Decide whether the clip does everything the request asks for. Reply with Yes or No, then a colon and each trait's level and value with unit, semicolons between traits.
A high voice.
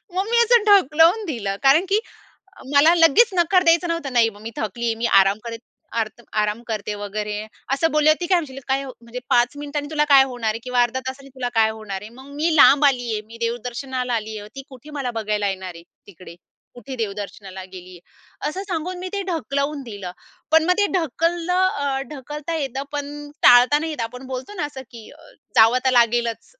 Yes: very high, 260 Hz